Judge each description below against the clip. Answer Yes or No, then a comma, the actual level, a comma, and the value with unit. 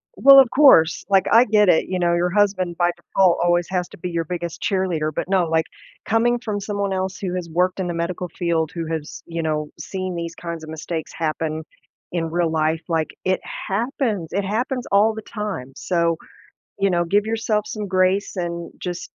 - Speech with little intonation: No, average, 3.3 semitones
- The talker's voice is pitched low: No, medium, 180 Hz